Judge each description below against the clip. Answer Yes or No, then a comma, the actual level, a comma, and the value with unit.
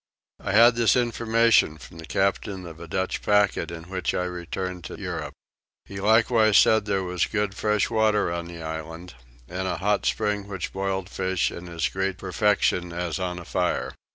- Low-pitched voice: Yes, very low, 95 Hz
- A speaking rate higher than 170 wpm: Yes, average, 180 wpm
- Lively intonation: No, average, 3.0 semitones